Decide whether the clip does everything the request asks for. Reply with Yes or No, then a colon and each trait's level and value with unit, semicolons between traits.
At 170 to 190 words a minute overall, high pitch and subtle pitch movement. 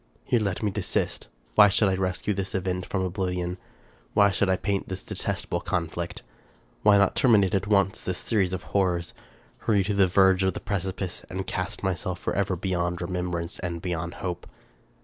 No: average, 185 wpm; very low, 95 Hz; narrow, 1.8 semitones